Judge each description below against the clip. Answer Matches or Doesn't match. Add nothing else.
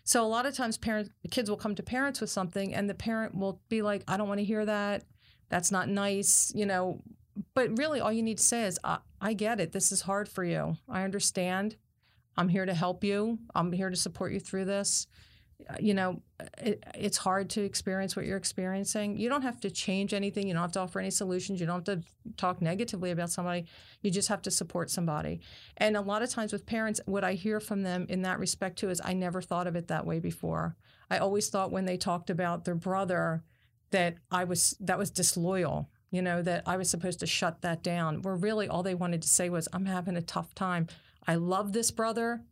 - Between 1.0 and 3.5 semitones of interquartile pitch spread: Matches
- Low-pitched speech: Doesn't match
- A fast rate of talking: Matches